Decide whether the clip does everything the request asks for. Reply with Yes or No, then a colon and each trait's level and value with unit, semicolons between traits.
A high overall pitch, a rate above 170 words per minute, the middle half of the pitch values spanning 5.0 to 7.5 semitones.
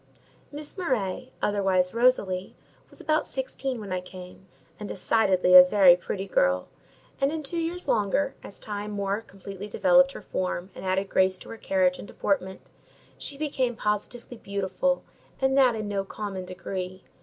No: high, 200 Hz; average, 160 wpm; wide, 5.5 semitones